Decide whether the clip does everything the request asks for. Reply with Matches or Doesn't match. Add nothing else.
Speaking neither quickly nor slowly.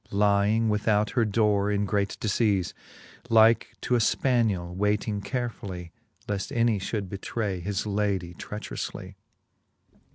Doesn't match